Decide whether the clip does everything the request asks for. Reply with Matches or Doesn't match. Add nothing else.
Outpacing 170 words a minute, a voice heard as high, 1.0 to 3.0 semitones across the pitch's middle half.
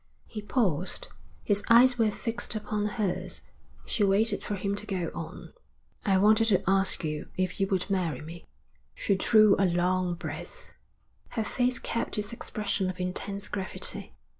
Doesn't match